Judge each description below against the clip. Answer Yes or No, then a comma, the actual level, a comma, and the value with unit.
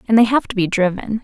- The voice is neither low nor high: No, high, 210 Hz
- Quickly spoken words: Yes, fast, 290 wpm